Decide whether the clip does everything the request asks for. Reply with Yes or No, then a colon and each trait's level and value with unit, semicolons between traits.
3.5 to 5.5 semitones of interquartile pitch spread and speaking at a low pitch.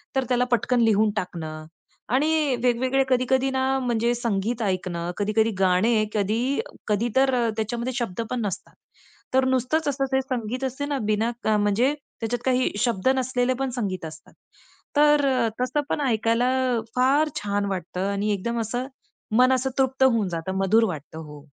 No: average, 4.1 semitones; high, 235 Hz